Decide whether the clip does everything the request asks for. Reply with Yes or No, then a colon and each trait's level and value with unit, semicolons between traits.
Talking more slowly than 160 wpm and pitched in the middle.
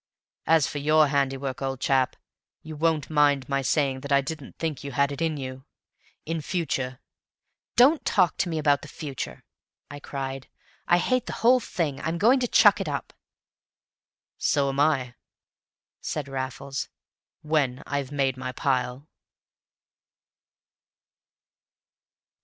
Yes: average, 140 wpm; medium, 145 Hz